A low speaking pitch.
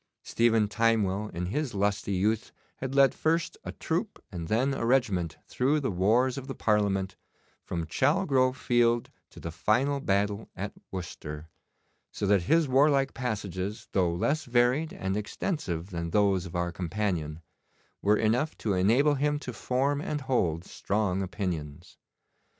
Yes: low, 105 Hz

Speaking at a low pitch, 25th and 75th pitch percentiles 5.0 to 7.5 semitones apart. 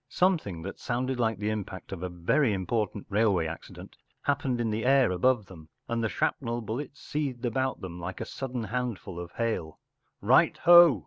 Yes: low, 115 Hz; wide, 5.4 semitones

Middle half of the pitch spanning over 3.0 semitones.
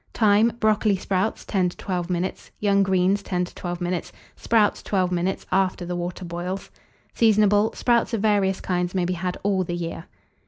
No: narrow, 2.4 semitones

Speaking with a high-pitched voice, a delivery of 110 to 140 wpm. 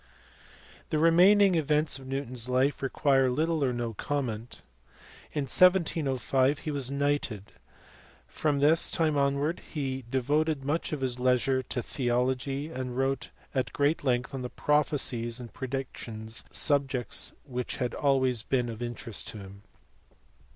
No: low, 135 Hz; slow, 135 wpm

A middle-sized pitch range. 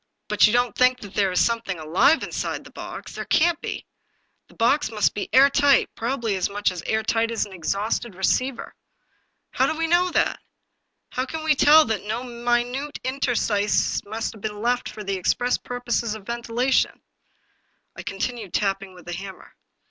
Yes: average, 3.9 semitones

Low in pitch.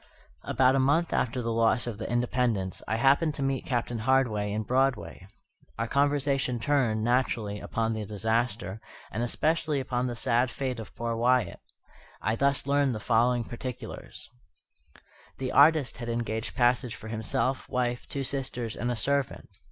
Yes: low, 120 Hz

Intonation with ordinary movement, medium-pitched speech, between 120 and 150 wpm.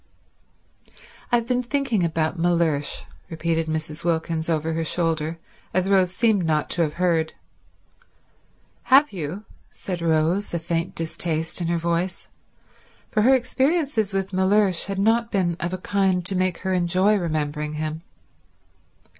Yes: average, 3.4 semitones; medium, 175 Hz; average, 140 wpm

